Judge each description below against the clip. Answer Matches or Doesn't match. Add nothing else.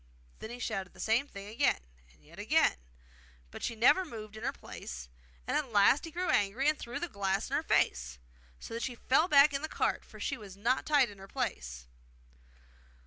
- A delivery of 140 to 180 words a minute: Doesn't match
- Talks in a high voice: Matches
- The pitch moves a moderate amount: Doesn't match